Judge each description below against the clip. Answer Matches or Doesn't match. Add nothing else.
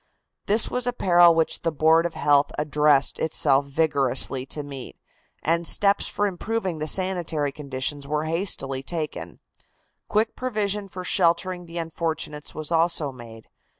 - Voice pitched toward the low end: Doesn't match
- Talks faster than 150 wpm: Doesn't match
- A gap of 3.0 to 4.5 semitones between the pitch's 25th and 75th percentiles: Matches